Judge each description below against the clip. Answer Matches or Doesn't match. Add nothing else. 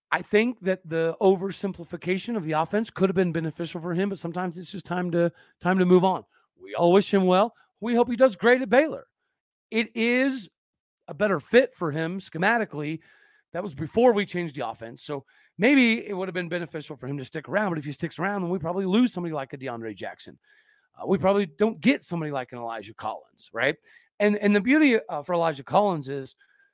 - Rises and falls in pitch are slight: Doesn't match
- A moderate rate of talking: Doesn't match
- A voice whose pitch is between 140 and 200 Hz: Matches